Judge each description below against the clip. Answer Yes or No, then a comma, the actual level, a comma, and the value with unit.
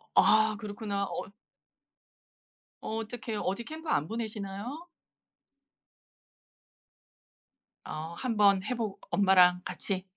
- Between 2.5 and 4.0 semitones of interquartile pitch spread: Yes, average, 2.9 semitones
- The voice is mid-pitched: No, high, 210 Hz